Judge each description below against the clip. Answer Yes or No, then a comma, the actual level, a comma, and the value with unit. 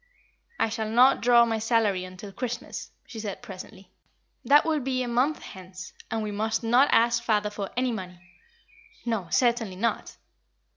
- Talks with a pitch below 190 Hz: No, high, 225 Hz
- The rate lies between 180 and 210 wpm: No, average, 160 wpm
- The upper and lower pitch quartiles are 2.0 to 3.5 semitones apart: Yes, average, 3.2 semitones